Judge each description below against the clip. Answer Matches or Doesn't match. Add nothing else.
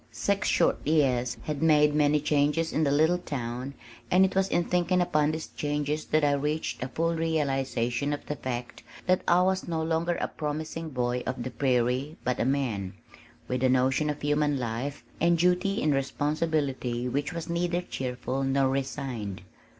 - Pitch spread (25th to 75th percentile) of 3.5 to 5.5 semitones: Matches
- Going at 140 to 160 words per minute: Doesn't match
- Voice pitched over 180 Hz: Doesn't match